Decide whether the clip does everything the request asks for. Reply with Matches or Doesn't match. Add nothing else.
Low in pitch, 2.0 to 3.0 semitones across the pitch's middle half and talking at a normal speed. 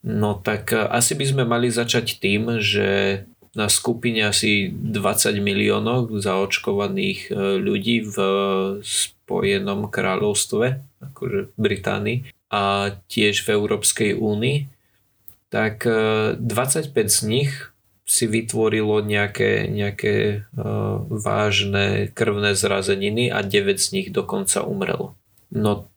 Doesn't match